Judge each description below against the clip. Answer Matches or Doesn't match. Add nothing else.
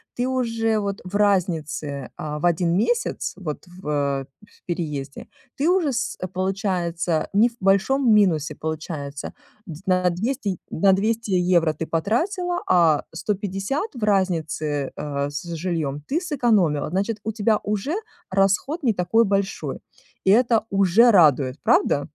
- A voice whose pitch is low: Doesn't match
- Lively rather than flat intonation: Matches